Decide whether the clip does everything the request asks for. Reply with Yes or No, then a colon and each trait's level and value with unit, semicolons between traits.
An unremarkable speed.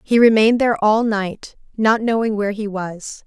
Yes: average, 185 wpm